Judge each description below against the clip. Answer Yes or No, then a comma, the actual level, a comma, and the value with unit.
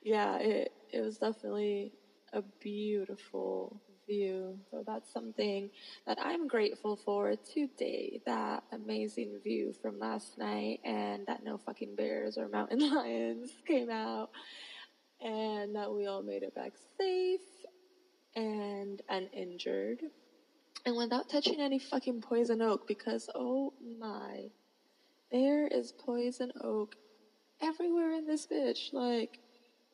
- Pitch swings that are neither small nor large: No, wide, 6.7 semitones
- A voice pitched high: Yes, high, 225 Hz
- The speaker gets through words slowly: Yes, slow, 120 wpm